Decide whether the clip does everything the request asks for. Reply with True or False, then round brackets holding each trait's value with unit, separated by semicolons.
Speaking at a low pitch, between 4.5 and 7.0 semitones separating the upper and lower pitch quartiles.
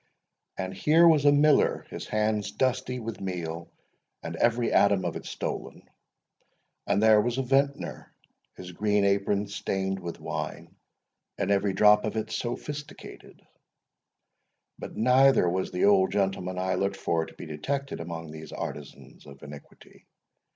True (100 Hz; 4.9 semitones)